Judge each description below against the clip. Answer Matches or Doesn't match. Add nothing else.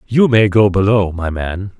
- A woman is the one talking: Doesn't match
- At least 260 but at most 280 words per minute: Doesn't match